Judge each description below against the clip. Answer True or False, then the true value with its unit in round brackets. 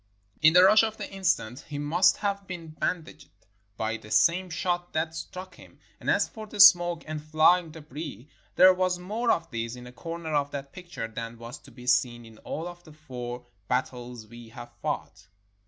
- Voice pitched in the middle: True (155 Hz)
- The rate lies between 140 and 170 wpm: False (190 wpm)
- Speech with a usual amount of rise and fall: False (6.4 semitones)